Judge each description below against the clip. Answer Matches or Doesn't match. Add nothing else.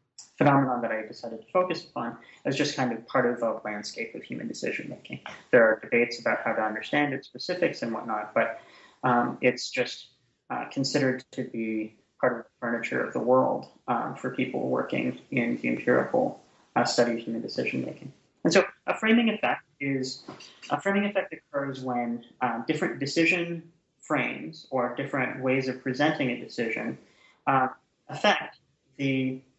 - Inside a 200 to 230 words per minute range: Doesn't match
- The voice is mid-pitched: Doesn't match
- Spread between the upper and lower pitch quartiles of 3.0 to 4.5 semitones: Matches